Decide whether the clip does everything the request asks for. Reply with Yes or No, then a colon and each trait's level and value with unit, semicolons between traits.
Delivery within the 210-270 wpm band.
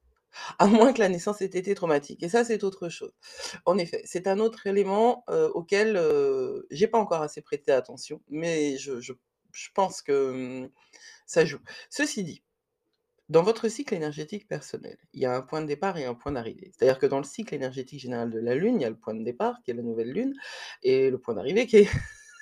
Yes: fast, 220 wpm